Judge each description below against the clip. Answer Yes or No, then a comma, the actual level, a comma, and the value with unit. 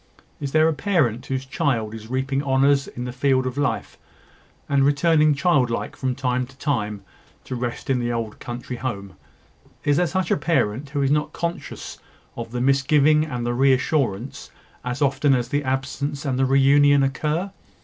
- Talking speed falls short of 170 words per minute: No, average, 180 wpm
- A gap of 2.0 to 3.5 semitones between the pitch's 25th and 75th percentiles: Yes, narrow, 2.6 semitones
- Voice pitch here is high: No, low, 135 Hz